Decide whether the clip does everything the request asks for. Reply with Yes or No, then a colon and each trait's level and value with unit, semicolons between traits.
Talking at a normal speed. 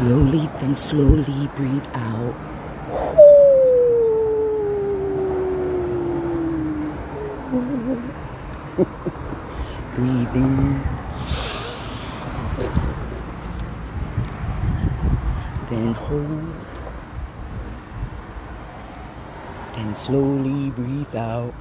No: slow, 35 wpm